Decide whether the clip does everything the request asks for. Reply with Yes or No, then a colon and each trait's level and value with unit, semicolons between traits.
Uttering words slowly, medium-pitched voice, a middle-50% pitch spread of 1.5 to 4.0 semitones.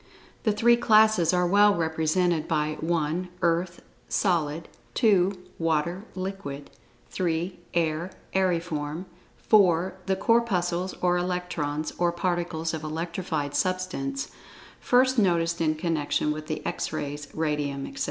Yes: slow, 120 wpm; medium, 170 Hz; average, 3.0 semitones